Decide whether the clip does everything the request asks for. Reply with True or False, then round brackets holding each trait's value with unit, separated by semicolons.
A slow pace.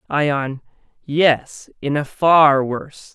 True (115 wpm)